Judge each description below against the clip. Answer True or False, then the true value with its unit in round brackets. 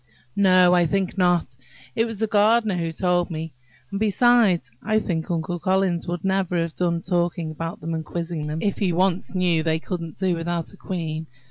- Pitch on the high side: False (175 Hz)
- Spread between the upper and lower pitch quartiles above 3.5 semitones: False (2.6 semitones)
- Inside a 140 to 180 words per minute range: False (195 wpm)